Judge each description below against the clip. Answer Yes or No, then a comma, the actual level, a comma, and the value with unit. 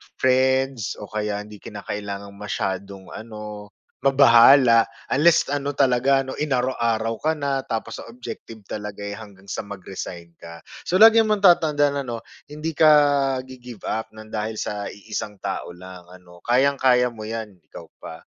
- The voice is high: No, low, 115 Hz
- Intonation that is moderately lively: Yes, average, 4.7 semitones